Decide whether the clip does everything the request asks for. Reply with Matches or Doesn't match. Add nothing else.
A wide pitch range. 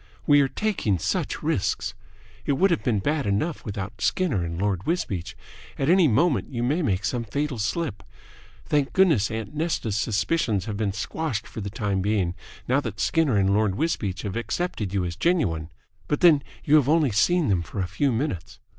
Matches